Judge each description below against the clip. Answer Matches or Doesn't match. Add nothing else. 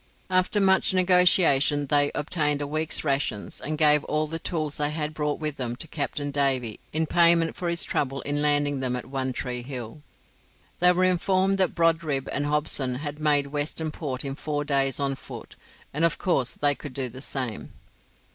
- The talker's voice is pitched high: Doesn't match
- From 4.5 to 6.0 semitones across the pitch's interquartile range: Doesn't match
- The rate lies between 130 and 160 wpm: Doesn't match